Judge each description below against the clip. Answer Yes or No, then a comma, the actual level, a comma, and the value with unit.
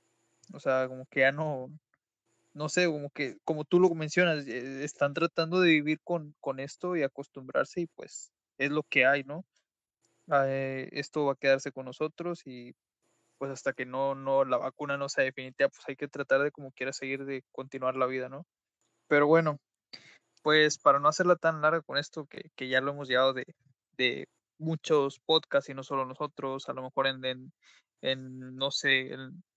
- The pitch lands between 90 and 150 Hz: Yes, medium, 140 Hz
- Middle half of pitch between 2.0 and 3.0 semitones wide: Yes, narrow, 2.6 semitones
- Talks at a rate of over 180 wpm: Yes, fast, 190 wpm